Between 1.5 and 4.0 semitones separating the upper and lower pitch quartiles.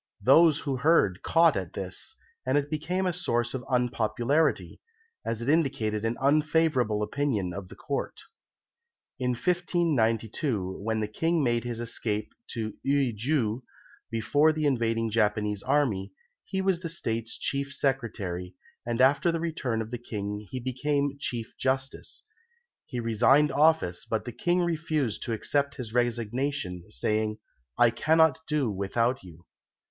No: average, 5.0 semitones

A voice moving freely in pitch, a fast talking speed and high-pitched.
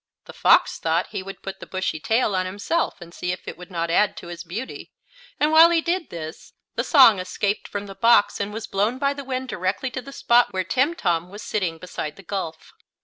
Yes: wide, 6.1 semitones; fast, 225 wpm; high, 200 Hz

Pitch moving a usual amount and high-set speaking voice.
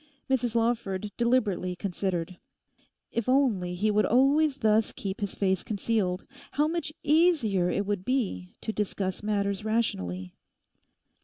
Yes: average, 4.4 semitones; high, 210 Hz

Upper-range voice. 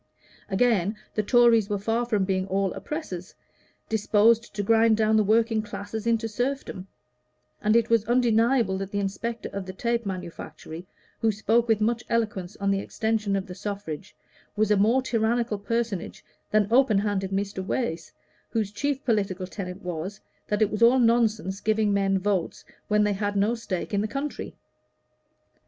Yes: high, 210 Hz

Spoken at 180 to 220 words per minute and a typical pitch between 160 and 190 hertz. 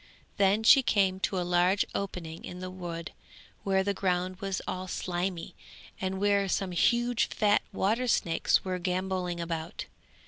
No: average, 150 wpm; medium, 185 Hz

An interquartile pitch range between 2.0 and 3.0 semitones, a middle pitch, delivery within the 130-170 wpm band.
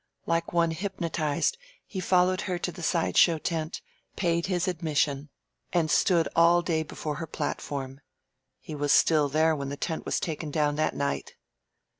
Yes: narrow, 2.6 semitones; medium, 160 Hz; average, 165 wpm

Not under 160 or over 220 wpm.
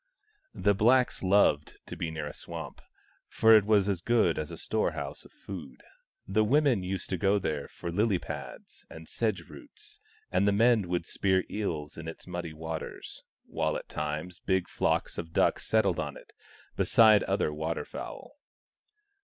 Yes: average, 170 wpm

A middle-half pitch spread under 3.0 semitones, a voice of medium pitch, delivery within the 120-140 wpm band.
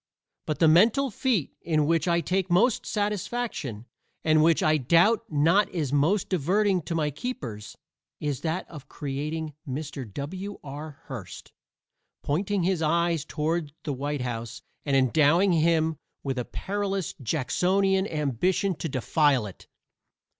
No: average, 4.8 semitones; medium, 160 Hz; slow, 135 wpm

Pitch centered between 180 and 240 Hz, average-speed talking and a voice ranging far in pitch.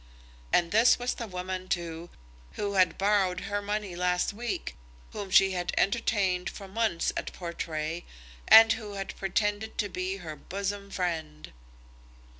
No: high, 190 Hz; average, 145 wpm; narrow, 2.5 semitones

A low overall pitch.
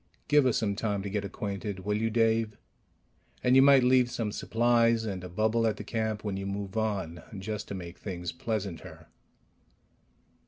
Yes: low, 105 Hz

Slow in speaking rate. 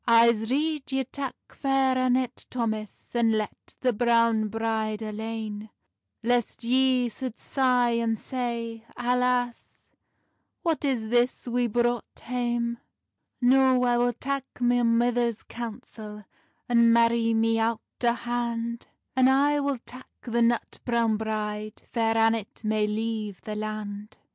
Yes: slow, 130 wpm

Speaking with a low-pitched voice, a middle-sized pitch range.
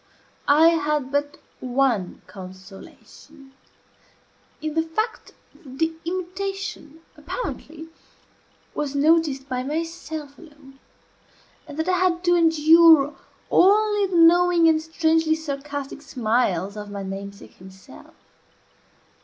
No: very high, 305 Hz; average, 3.7 semitones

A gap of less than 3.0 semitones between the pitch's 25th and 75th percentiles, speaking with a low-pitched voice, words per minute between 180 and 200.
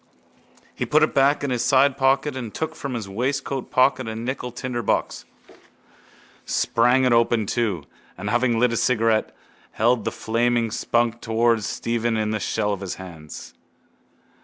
No: narrow, 2.6 semitones; low, 120 Hz; average, 150 wpm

